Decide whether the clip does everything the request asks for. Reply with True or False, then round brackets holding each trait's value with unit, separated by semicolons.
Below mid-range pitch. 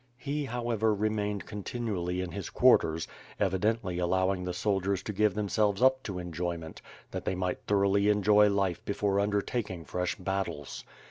True (100 Hz)